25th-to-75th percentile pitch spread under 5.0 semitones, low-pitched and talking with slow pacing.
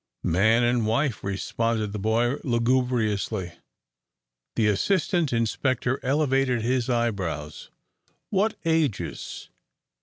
Yes: average, 3.5 semitones; low, 120 Hz; slow, 90 wpm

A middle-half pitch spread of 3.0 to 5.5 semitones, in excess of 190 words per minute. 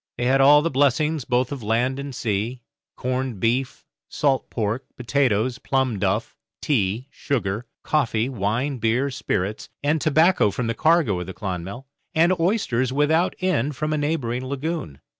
No: average, 4.4 semitones; average, 155 wpm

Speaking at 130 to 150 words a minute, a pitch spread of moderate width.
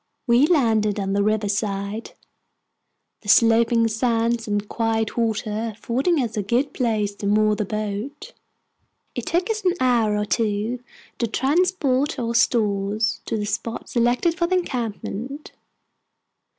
Yes: average, 140 wpm; average, 3.2 semitones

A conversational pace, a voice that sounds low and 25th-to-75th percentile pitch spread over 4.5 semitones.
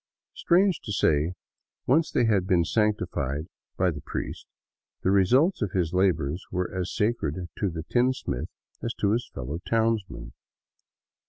Yes: average, 145 wpm; very low, 95 Hz; wide, 5.4 semitones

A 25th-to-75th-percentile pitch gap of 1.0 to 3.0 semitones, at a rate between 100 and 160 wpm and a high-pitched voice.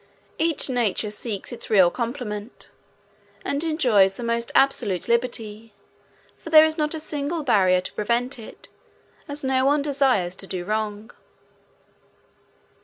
No: average, 5.2 semitones; slow, 135 wpm; high, 235 Hz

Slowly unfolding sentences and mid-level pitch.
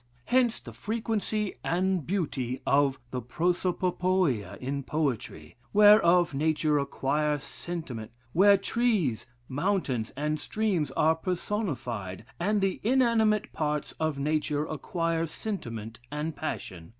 Yes: slow, 95 wpm; medium, 160 Hz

